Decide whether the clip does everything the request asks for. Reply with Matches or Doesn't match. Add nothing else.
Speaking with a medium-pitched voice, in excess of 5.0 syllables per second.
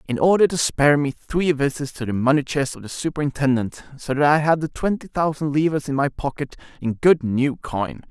Matches